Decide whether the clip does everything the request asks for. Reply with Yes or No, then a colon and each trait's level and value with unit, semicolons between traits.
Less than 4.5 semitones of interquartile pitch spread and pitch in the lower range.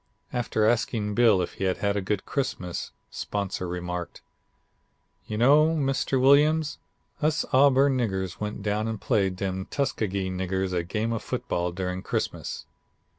No: wide, 5.6 semitones; low, 105 Hz